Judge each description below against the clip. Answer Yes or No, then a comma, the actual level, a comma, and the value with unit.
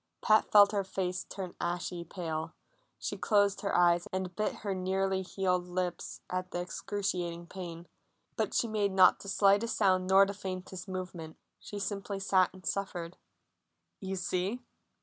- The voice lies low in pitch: No, medium, 185 Hz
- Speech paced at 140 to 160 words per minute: Yes, average, 155 wpm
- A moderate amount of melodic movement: No, narrow, 1.8 semitones